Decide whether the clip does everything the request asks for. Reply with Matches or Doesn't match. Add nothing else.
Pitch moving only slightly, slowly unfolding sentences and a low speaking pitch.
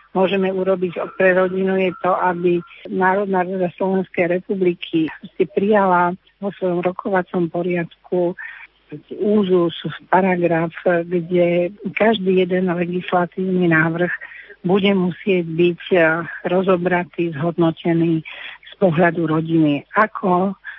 Doesn't match